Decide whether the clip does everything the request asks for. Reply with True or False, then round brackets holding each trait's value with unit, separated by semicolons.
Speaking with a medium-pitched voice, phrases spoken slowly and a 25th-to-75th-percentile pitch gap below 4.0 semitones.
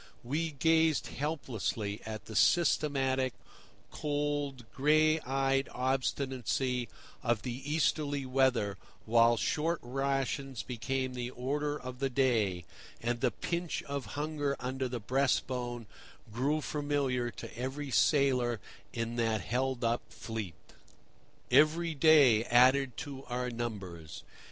False (130 Hz; 115 wpm; 3.3 semitones)